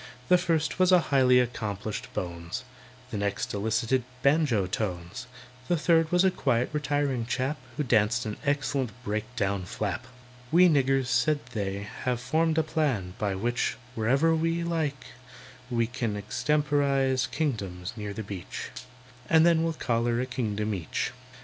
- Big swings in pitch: Yes, wide, 6.0 semitones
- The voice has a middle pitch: No, low, 125 Hz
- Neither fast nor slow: Yes, average, 150 wpm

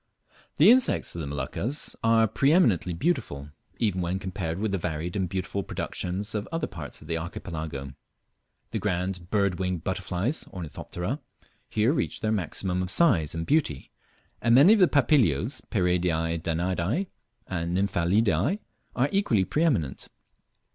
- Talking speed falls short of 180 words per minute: Yes, average, 145 wpm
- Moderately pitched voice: No, very low, 95 Hz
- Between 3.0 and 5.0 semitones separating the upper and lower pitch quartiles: No, wide, 5.4 semitones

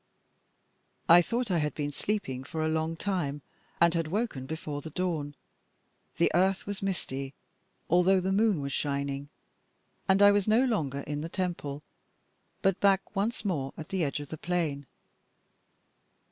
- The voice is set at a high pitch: No, medium, 165 Hz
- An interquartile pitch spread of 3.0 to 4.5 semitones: No, average, 4.9 semitones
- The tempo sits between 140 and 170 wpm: Yes, average, 160 wpm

